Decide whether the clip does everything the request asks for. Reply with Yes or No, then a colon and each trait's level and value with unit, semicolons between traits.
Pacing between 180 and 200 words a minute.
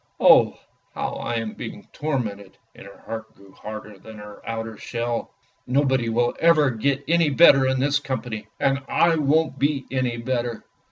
No: average, 170 wpm